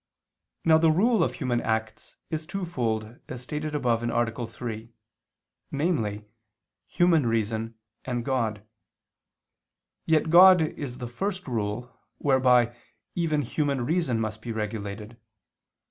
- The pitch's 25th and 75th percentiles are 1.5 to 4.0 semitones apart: No, wide, 5.5 semitones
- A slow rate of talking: Yes, slow, 115 wpm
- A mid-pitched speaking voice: No, low, 125 Hz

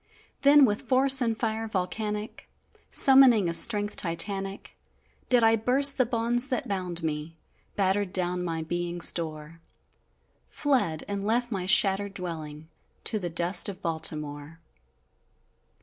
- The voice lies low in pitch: No, high, 195 Hz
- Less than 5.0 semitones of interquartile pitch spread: No, average, 5.3 semitones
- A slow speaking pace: Yes, slow, 130 wpm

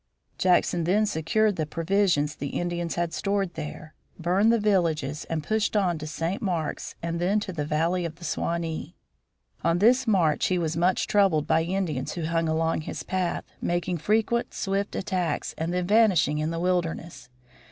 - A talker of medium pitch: Yes, medium, 175 Hz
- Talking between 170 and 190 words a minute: Yes, average, 175 wpm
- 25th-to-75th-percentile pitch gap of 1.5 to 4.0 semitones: Yes, average, 3.3 semitones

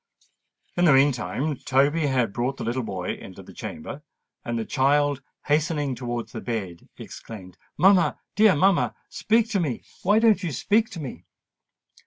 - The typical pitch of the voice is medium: Yes, medium, 145 Hz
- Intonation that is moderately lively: No, wide, 6.7 semitones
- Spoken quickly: No, average, 145 wpm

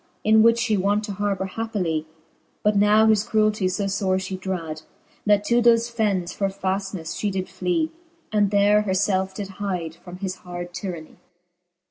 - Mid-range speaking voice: No, high, 200 Hz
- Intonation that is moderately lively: No, narrow, 2.2 semitones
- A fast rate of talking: No, average, 170 wpm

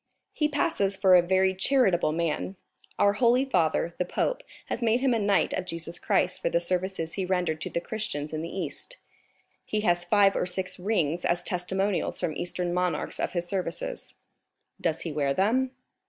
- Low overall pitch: No, medium, 185 Hz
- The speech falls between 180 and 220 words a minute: Yes, average, 185 wpm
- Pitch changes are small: No, average, 3.2 semitones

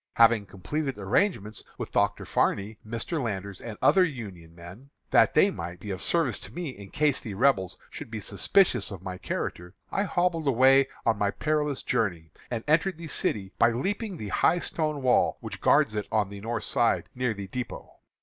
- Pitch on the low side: Yes, low, 115 Hz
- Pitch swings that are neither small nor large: No, wide, 6.8 semitones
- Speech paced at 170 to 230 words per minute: Yes, average, 190 wpm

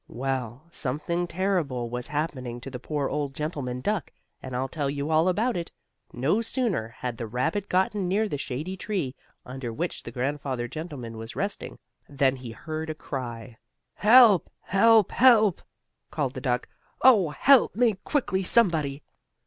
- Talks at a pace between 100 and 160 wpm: Yes, average, 155 wpm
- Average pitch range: No, wide, 6.9 semitones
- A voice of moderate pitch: Yes, medium, 150 Hz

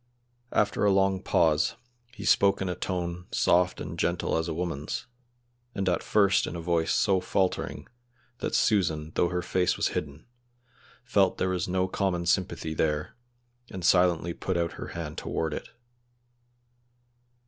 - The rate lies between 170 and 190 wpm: No, average, 155 wpm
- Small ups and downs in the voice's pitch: Yes, narrow, 2.2 semitones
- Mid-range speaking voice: No, very low, 90 Hz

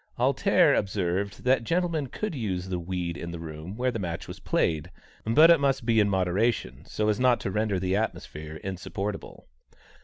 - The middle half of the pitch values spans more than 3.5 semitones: Yes, average, 5.0 semitones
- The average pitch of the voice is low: Yes, low, 100 Hz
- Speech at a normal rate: Yes, average, 180 wpm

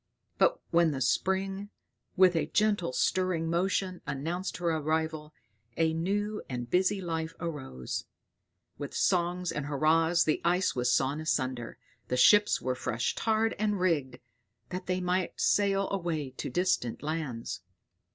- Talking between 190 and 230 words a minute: No, average, 140 wpm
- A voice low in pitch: No, medium, 170 Hz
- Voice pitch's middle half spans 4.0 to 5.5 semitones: Yes, average, 4.3 semitones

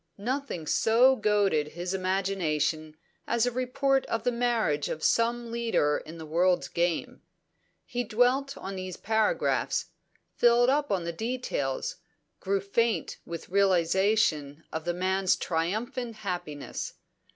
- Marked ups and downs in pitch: Yes, wide, 5.8 semitones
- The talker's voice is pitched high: Yes, high, 195 Hz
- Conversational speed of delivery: No, slow, 125 wpm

